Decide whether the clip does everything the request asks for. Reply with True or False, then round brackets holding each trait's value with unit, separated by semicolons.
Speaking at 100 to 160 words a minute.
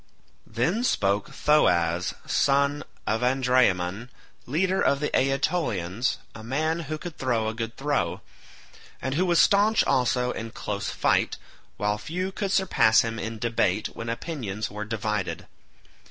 True (140 wpm)